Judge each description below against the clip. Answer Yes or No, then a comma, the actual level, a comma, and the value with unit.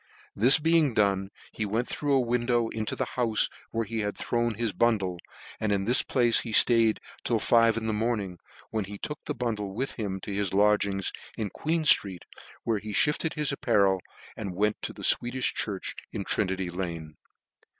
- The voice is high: No, low, 110 Hz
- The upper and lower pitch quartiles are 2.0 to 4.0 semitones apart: Yes, average, 3.2 semitones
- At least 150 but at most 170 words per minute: No, average, 185 wpm